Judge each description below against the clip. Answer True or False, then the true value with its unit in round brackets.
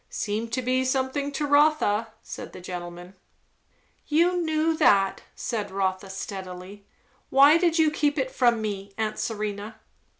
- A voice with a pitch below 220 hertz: False (225 Hz)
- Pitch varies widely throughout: True (6.6 semitones)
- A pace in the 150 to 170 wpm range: False (140 wpm)